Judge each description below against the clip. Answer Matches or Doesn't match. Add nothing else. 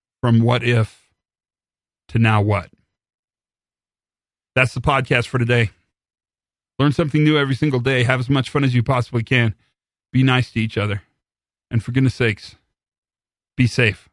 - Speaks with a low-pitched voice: Matches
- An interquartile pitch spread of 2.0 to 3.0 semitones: Matches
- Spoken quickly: Doesn't match